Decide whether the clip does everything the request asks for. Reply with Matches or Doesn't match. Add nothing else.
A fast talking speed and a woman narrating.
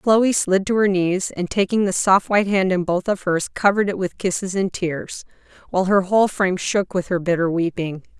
Matches